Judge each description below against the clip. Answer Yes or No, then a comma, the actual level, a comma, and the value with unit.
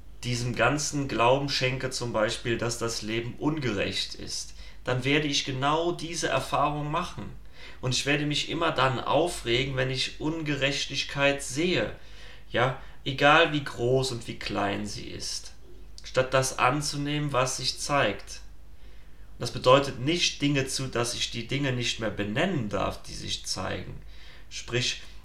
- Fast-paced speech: No, average, 145 wpm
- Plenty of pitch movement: No, average, 3.5 semitones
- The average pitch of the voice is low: Yes, low, 130 Hz